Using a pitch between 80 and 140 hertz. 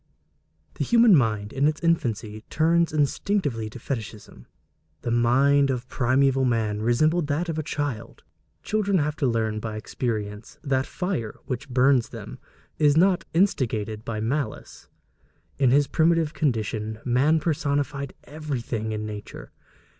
Yes: low, 135 Hz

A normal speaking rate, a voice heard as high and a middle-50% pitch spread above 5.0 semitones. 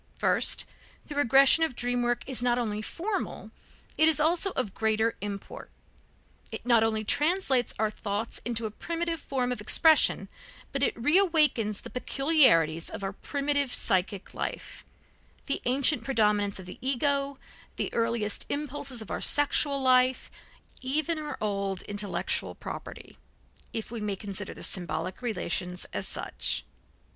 Yes: average, 145 wpm; high, 245 Hz; wide, 5.4 semitones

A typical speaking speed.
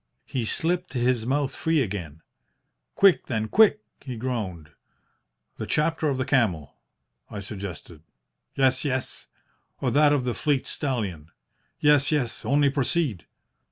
No: slow, 130 wpm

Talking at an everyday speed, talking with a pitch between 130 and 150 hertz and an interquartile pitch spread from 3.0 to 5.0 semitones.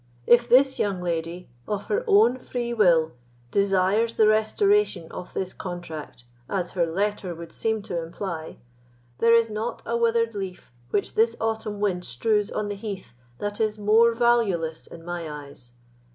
No: average, 160 wpm; high, 205 Hz; average, 4.6 semitones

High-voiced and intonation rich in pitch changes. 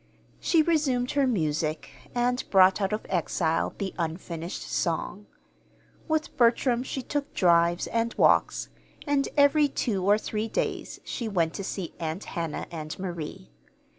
Yes: high, 200 Hz; wide, 6.8 semitones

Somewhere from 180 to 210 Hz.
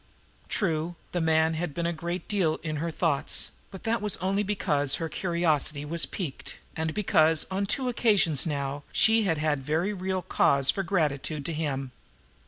No: medium, 165 Hz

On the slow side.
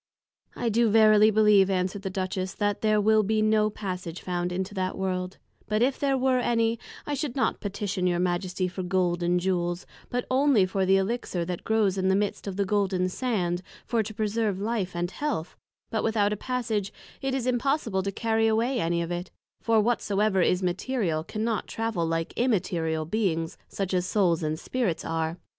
No: average, 190 wpm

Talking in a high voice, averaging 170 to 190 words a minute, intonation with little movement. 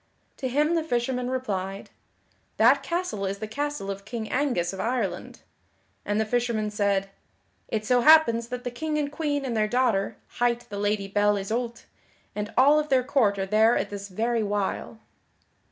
No: high, 230 Hz; average, 175 wpm; average, 4.1 semitones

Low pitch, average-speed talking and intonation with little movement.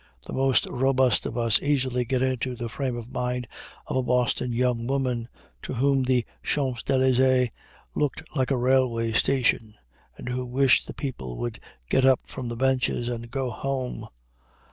Yes: low, 125 Hz; average, 165 wpm; narrow, 1.7 semitones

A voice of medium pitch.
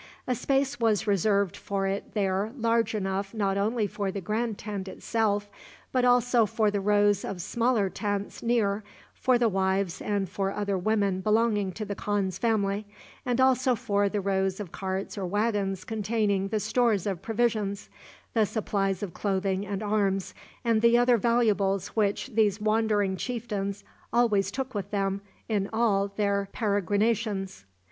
No: high, 205 Hz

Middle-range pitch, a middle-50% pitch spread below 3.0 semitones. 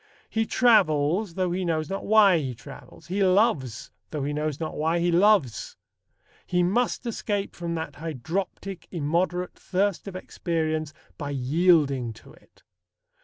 No: medium, 170 Hz; average, 4.2 semitones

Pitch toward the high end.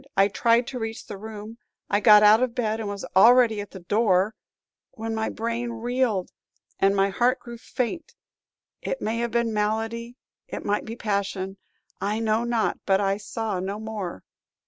Yes: high, 220 Hz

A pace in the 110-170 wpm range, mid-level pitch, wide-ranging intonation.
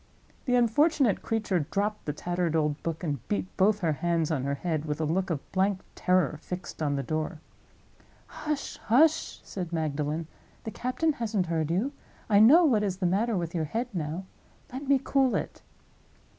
No: average, 180 wpm; medium, 180 Hz; wide, 6.2 semitones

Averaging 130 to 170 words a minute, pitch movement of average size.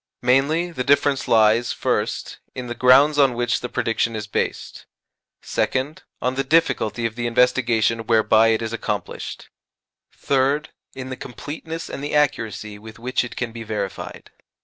Yes: average, 155 wpm; average, 3.3 semitones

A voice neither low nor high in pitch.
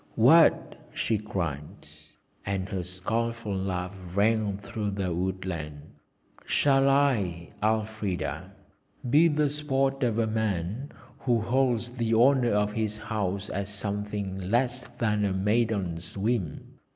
No: low, 105 Hz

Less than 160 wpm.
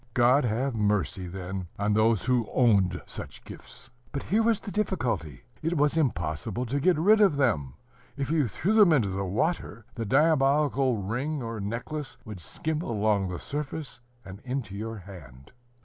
No: average, 165 wpm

